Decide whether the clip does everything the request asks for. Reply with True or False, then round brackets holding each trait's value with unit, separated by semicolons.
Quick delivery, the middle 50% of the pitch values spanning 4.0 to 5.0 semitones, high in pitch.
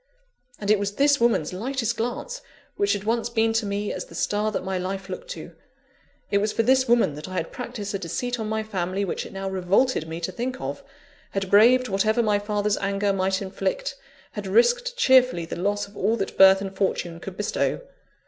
False (210 wpm; 3.6 semitones; 205 Hz)